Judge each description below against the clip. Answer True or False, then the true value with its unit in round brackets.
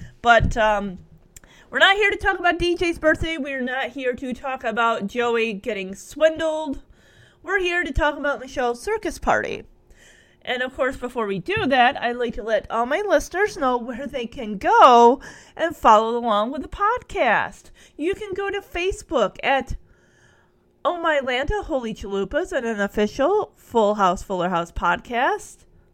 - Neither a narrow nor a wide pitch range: False (6.1 semitones)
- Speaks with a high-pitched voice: True (265 Hz)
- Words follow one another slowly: False (165 wpm)